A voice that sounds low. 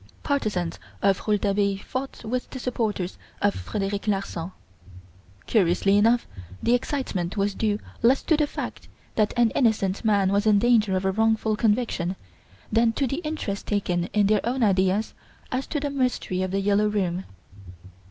No: high, 210 Hz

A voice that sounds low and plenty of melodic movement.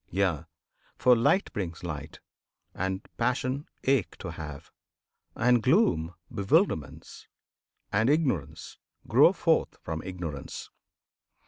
Yes: very low, 95 Hz; wide, 7.9 semitones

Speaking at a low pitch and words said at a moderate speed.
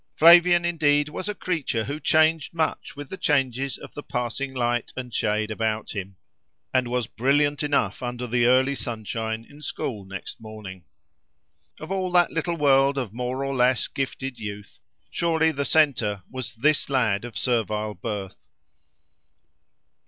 Yes: low, 130 Hz; average, 150 wpm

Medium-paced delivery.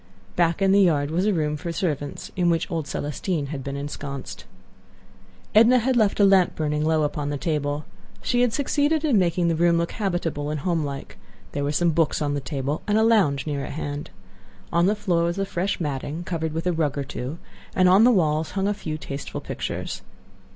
No: fast, 210 wpm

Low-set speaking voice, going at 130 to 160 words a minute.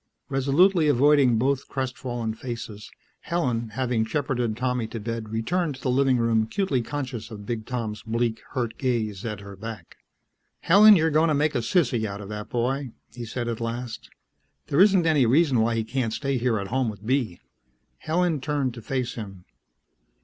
No: low, 120 Hz; average, 180 wpm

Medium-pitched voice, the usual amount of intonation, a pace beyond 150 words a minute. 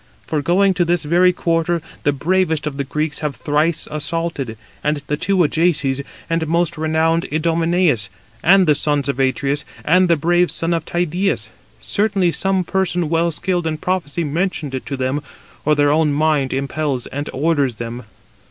Yes: medium, 160 Hz; average, 3.2 semitones; average, 165 wpm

